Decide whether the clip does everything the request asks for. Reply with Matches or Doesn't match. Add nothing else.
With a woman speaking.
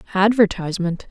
Matches